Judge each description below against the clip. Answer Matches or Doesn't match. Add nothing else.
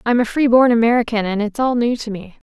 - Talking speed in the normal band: Doesn't match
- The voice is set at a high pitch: Matches